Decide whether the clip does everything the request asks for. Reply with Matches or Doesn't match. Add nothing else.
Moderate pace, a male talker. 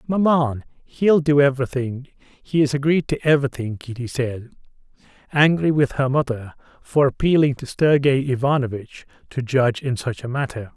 Matches